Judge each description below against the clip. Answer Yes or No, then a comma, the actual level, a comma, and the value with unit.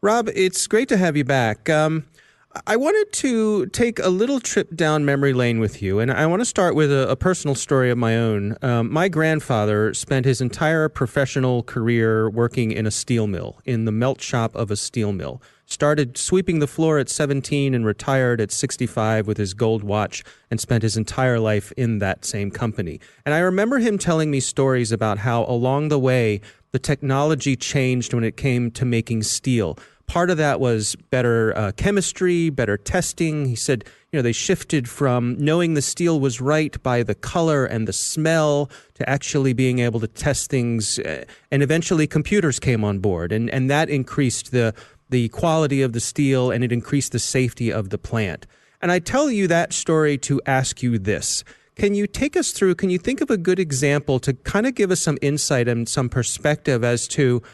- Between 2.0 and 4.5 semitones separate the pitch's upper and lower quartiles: No, average, 5.2 semitones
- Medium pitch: No, low, 130 Hz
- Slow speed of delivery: No, average, 200 wpm